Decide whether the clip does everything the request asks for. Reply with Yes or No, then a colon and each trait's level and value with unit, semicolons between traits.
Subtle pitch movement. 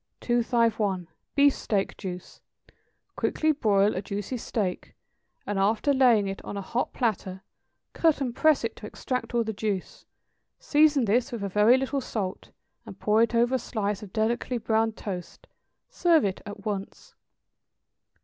No: average, 3.8 semitones